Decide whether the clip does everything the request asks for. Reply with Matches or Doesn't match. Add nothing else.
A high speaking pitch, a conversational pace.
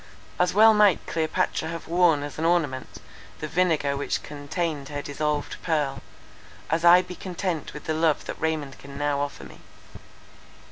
Doesn't match